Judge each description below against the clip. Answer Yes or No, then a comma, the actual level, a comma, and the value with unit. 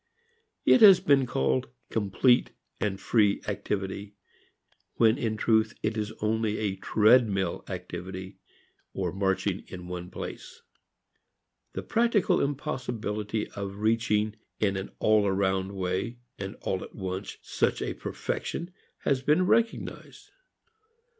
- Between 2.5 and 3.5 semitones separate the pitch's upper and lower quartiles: Yes, average, 3.0 semitones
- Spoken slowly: Yes, slow, 120 wpm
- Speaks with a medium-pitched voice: No, low, 105 Hz